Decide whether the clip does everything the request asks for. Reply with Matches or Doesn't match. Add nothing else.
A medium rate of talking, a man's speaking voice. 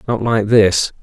Matches